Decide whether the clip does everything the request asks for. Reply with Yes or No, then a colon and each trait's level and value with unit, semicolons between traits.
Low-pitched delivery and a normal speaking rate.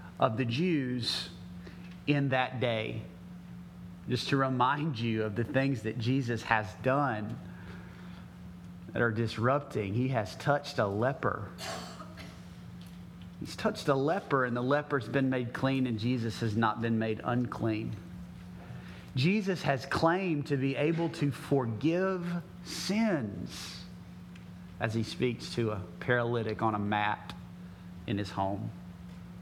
No: low, 115 Hz; slow, 130 wpm